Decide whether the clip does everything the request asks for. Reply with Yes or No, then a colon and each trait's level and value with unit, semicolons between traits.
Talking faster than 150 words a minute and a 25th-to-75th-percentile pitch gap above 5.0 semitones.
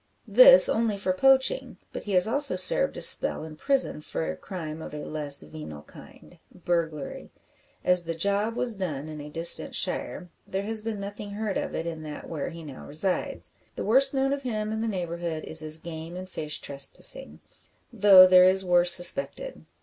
Yes: average, 190 wpm; wide, 5.4 semitones